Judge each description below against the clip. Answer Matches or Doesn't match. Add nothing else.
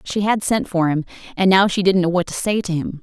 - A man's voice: Doesn't match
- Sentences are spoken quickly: Matches